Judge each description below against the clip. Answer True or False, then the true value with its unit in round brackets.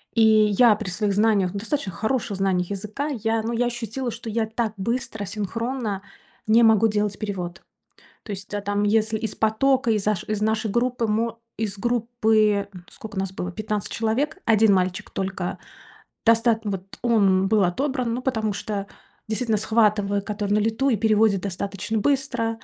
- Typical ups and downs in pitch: False (2.3 semitones)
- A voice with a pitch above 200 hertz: True (215 Hz)